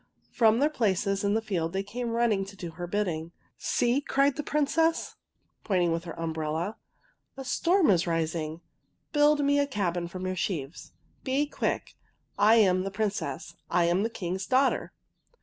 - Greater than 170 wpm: Yes, average, 180 wpm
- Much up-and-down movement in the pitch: Yes, wide, 6.7 semitones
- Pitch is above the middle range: Yes, high, 200 Hz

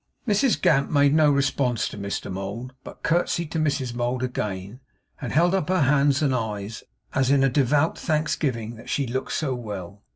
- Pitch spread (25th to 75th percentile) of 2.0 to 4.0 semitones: No, average, 4.4 semitones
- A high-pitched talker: No, low, 135 Hz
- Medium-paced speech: Yes, average, 185 wpm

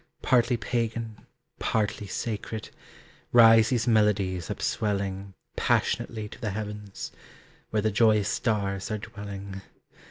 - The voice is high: No, low, 105 Hz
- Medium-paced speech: No, slow, 105 wpm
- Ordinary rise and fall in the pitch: No, narrow, 2.1 semitones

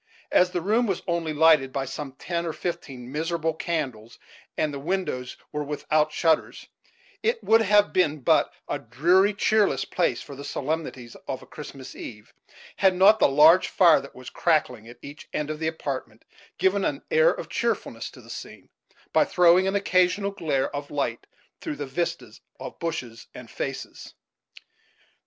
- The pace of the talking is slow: No, average, 170 wpm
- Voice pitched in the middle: Yes, medium, 160 Hz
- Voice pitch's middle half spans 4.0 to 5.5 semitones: Yes, average, 4.9 semitones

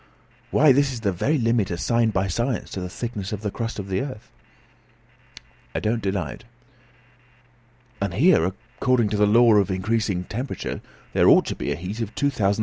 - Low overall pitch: Yes, low, 110 Hz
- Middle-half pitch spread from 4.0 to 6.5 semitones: No, average, 3.6 semitones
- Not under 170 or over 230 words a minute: Yes, average, 190 wpm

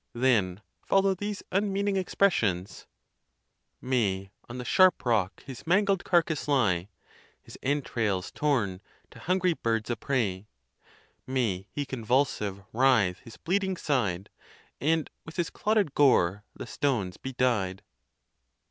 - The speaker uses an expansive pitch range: Yes, wide, 8.6 semitones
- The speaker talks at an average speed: No, slow, 125 wpm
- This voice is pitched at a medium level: No, low, 125 Hz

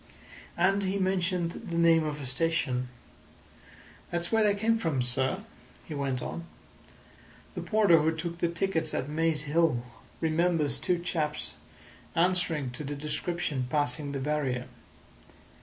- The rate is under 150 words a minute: Yes, average, 140 wpm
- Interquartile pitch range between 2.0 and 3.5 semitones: Yes, average, 3.1 semitones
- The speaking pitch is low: No, medium, 160 Hz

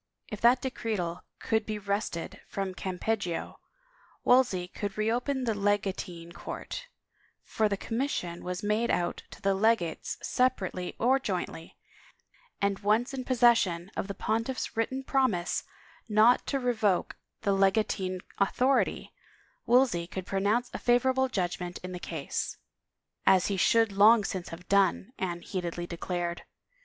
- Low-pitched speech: No, high, 200 Hz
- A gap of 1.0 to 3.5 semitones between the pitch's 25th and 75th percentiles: No, average, 4.6 semitones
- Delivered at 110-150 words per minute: Yes, average, 145 wpm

